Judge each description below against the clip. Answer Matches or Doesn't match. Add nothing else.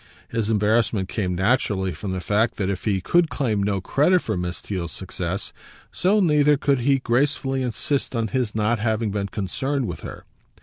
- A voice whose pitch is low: Matches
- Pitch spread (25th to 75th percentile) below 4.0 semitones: Doesn't match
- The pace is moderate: Matches